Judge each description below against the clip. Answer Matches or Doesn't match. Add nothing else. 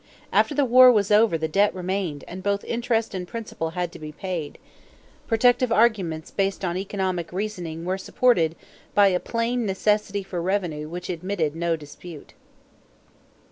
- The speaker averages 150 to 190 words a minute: Matches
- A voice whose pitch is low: Doesn't match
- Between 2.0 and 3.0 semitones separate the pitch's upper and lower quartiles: Doesn't match